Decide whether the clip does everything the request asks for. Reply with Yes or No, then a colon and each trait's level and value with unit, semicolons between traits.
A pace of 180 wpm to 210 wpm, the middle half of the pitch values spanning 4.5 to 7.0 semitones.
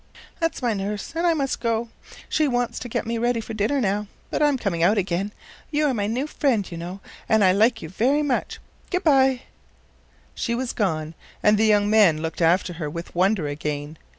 Yes: fast, 205 wpm; wide, 5.5 semitones